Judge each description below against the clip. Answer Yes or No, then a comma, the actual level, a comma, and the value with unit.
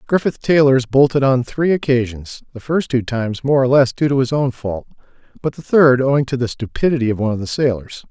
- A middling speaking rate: No, fast, 220 wpm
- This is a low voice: Yes, low, 130 Hz